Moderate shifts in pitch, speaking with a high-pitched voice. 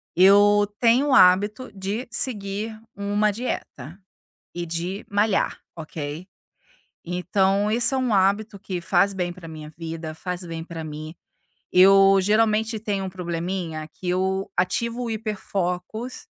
Yes: average, 3.3 semitones; high, 195 Hz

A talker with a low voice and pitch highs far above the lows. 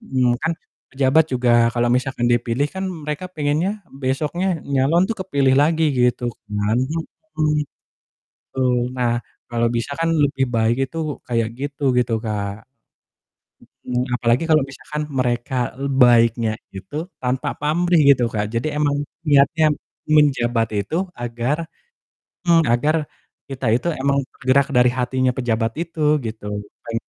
No: low, 130 Hz; average, 3.8 semitones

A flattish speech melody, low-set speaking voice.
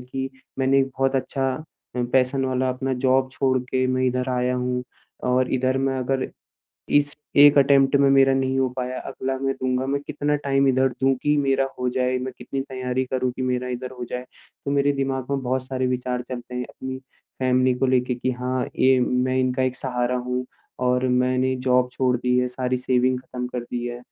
Yes: narrow, 0.9 semitones; low, 130 Hz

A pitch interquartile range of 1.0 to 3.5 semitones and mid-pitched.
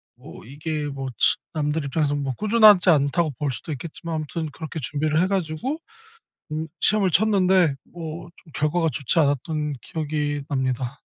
Yes: average, 2.9 semitones; medium, 155 Hz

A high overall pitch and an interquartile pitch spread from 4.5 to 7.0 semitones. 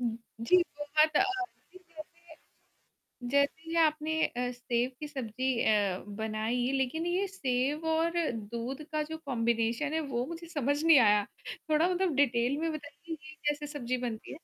Yes: very high, 285 Hz; average, 4.9 semitones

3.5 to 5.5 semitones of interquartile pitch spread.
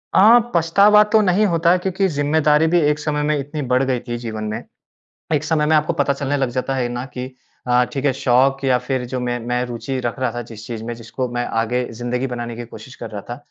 Yes: average, 3.8 semitones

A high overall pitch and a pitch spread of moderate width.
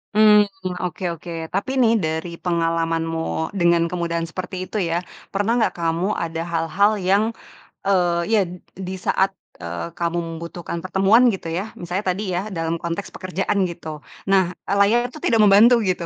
No: medium, 175 Hz; average, 3.3 semitones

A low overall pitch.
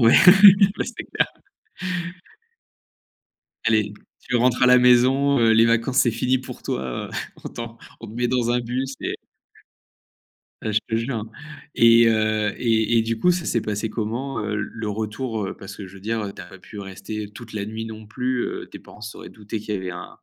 Yes: low, 115 Hz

